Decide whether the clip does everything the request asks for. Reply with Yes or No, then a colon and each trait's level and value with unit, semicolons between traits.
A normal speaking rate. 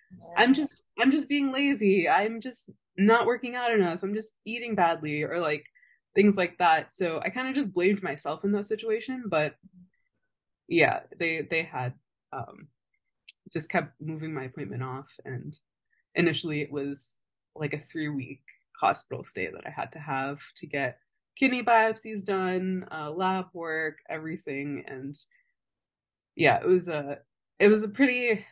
Yes: average, 160 wpm